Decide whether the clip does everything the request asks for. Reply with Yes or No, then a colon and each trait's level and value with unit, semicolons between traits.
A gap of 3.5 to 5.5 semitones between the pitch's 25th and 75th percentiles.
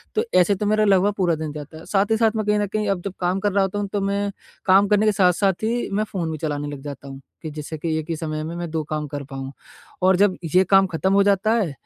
Yes: average, 4.4 semitones